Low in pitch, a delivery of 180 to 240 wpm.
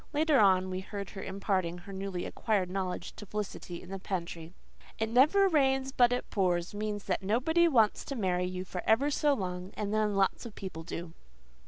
No: high, 200 Hz; average, 195 wpm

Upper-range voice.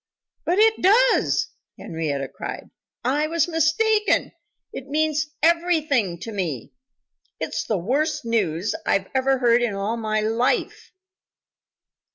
Yes: very high, 260 Hz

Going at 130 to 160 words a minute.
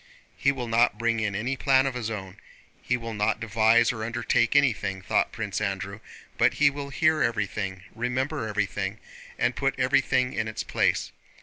No: average, 175 wpm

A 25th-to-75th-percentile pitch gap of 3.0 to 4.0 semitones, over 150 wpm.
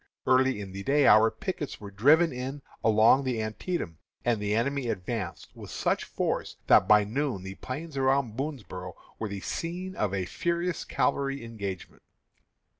No: average, 5.3 semitones; average, 160 wpm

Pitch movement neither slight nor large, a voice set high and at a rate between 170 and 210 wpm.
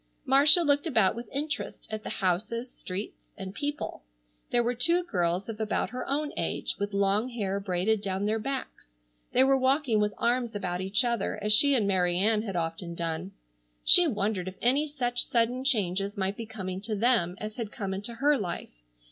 Yes: average, 4.8 semitones; high, 215 Hz; average, 190 wpm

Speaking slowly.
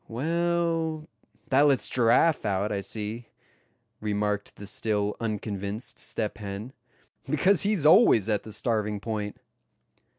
Yes: slow, 120 wpm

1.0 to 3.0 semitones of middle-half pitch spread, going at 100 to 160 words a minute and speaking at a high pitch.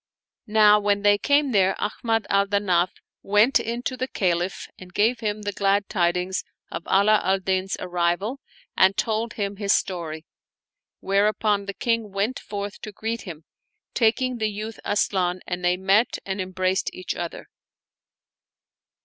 Yes: narrow, 2.5 semitones; average, 150 wpm; high, 200 Hz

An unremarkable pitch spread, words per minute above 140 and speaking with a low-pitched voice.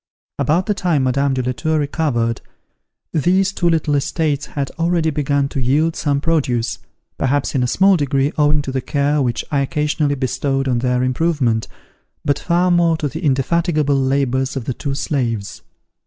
No: average, 3.3 semitones; average, 170 wpm; medium, 145 Hz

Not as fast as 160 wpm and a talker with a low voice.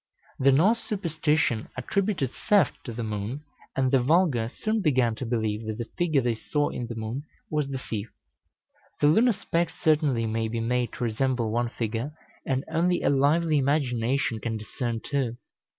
No: average, 170 wpm; low, 130 Hz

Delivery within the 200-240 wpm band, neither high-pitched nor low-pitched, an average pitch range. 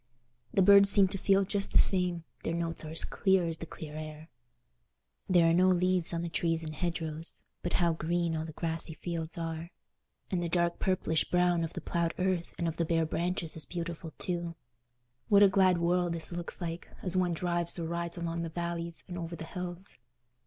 No: fast, 205 wpm; medium, 170 Hz; narrow, 1.5 semitones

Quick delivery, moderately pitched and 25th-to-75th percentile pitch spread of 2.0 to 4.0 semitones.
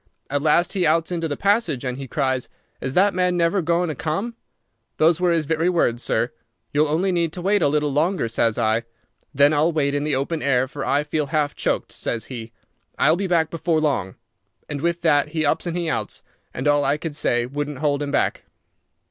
Yes: fast, 215 wpm; medium, 150 Hz; average, 3.2 semitones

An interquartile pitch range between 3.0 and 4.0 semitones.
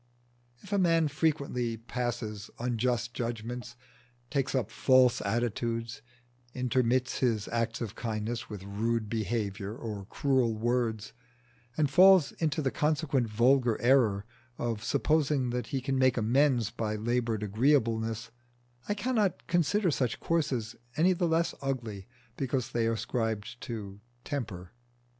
Yes: average, 3.5 semitones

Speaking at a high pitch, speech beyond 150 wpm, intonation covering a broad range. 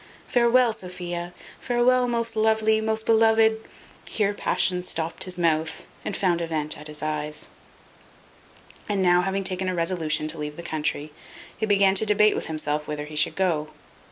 No: medium, 180 Hz; average, 170 wpm; wide, 5.9 semitones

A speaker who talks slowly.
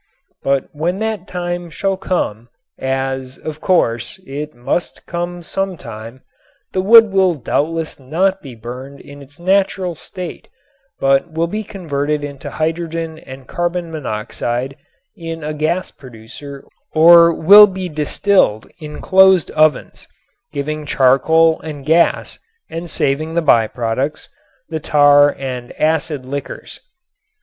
Yes: slow, 130 wpm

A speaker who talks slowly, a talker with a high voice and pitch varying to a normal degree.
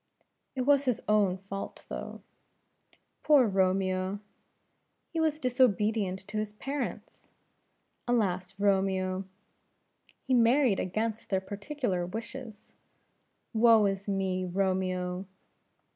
Yes: slow, 100 wpm; high, 200 Hz; average, 3.9 semitones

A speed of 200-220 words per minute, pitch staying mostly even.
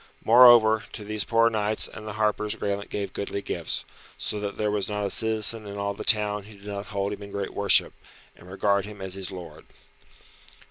Yes: fast, 205 wpm; narrow, 1.2 semitones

